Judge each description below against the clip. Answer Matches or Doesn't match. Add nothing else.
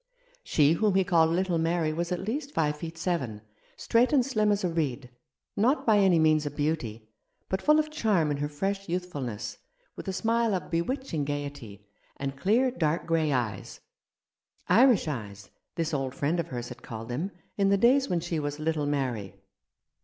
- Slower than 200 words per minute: Matches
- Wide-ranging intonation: Matches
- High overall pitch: Doesn't match